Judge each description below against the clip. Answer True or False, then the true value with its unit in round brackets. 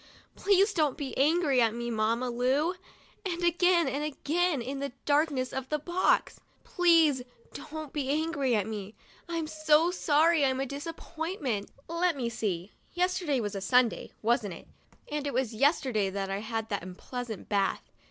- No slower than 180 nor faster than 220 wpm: False (170 wpm)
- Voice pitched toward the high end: True (280 Hz)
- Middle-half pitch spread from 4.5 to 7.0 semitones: True (5.6 semitones)